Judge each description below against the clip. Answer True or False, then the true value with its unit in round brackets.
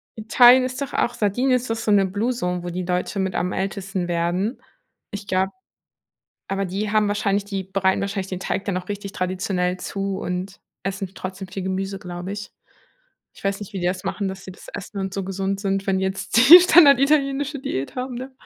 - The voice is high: True (195 Hz)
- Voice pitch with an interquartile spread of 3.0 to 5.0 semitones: False (2.5 semitones)